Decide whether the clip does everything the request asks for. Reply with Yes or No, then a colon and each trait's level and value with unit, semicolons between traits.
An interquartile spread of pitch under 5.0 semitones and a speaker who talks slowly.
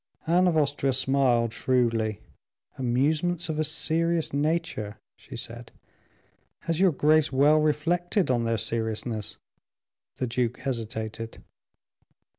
No: average, 5.3 semitones; slow, 110 wpm